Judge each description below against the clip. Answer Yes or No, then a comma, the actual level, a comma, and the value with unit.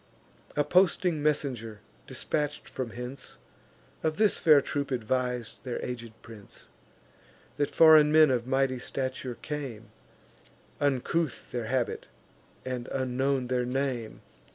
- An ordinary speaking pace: No, slow, 115 wpm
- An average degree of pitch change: Yes, average, 3.2 semitones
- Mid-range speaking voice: No, low, 130 Hz